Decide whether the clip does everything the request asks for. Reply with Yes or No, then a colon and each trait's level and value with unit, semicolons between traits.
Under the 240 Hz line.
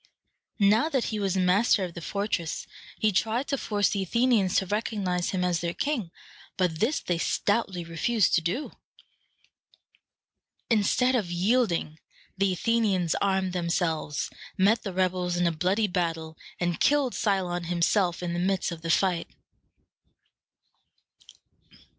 Yes: medium, 185 Hz